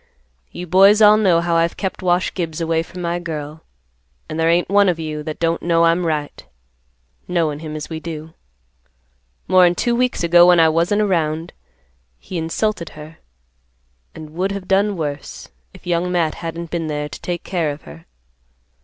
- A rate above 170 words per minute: Yes, average, 180 wpm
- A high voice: No, medium, 170 Hz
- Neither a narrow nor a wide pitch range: No, narrow, 2.2 semitones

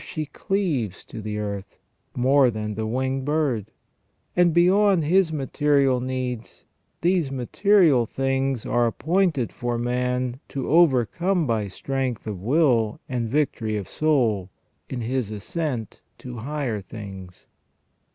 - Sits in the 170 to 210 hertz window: No, low, 130 Hz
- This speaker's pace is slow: Yes, slow, 125 wpm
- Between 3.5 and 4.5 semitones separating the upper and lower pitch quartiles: No, average, 5.3 semitones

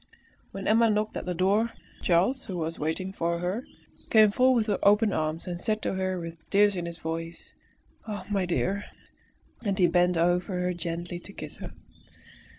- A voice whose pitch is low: No, medium, 185 Hz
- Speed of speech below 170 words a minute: No, average, 180 wpm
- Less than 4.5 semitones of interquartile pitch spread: Yes, average, 3.3 semitones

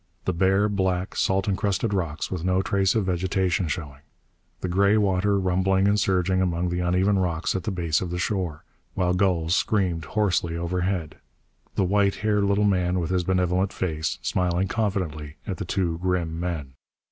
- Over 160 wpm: Yes, average, 170 wpm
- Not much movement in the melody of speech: Yes, narrow, 2.0 semitones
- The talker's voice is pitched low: Yes, very low, 95 Hz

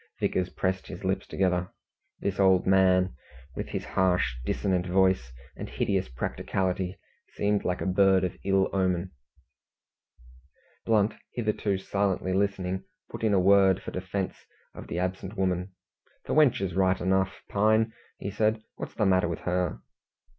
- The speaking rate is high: No, average, 145 wpm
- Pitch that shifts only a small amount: Yes, narrow, 1.4 semitones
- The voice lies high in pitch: No, very low, 95 Hz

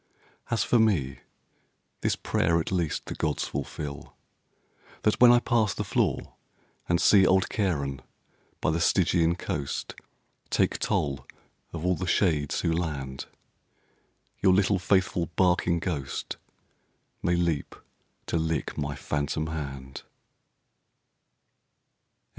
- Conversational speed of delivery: No, slow, 120 wpm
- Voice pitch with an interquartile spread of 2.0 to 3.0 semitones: No, average, 4.2 semitones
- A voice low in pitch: Yes, very low, 85 Hz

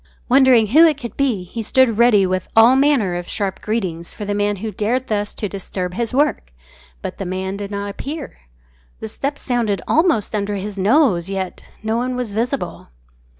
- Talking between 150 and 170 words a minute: No, average, 190 wpm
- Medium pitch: No, high, 215 Hz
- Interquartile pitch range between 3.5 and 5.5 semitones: Yes, average, 4.3 semitones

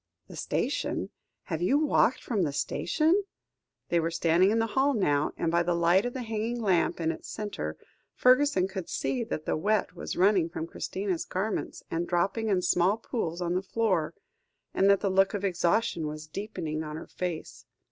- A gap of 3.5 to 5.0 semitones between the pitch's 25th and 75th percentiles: Yes, average, 4.6 semitones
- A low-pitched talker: No, high, 190 Hz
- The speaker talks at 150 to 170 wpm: No, average, 190 wpm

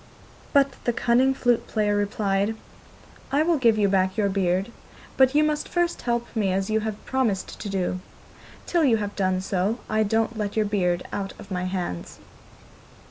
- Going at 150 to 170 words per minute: No, average, 180 wpm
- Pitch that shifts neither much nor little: Yes, average, 3.7 semitones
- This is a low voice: No, high, 210 Hz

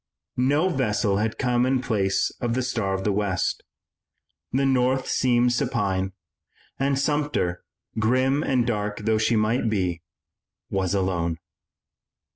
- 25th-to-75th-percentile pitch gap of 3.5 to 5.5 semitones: Yes, average, 4.7 semitones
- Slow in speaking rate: Yes, slow, 130 wpm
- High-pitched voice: No, low, 115 Hz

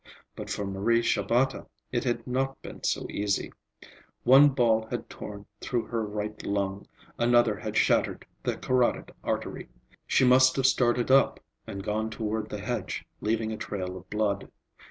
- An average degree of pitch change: Yes, average, 3.1 semitones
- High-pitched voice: No, low, 110 Hz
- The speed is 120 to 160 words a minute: Yes, average, 155 wpm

